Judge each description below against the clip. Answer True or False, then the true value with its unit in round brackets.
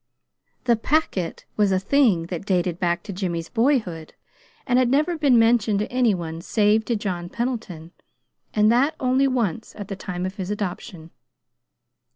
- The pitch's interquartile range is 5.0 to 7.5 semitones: True (5.4 semitones)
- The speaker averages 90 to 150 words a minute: False (165 wpm)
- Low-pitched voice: False (210 Hz)